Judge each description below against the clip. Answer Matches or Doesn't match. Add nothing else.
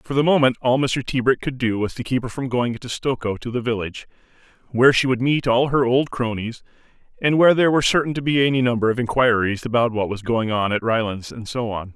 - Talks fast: Matches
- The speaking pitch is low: Matches